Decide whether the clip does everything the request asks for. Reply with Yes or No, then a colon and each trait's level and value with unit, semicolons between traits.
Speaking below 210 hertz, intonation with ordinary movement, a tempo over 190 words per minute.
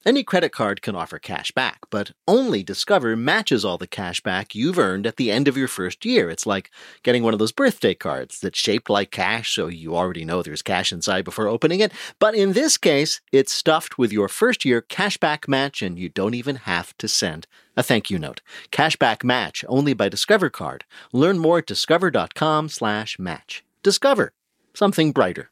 No: low, 135 Hz; wide, 8.4 semitones; average, 200 wpm